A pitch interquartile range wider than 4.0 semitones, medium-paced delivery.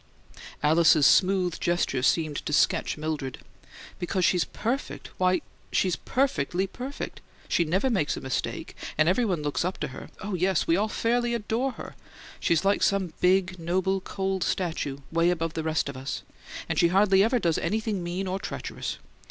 No: average, 3.4 semitones; average, 170 wpm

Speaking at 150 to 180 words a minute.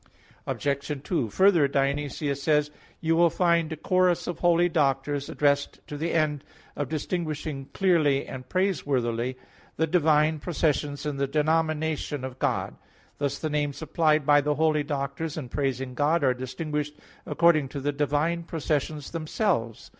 Yes: average, 155 wpm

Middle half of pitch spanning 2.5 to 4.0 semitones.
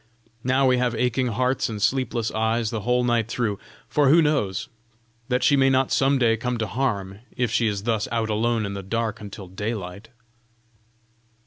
Yes: average, 3.0 semitones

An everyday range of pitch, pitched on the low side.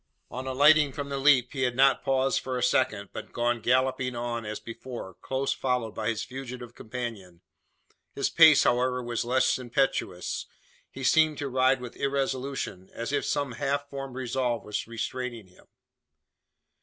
No: narrow, 2.2 semitones; low, 130 Hz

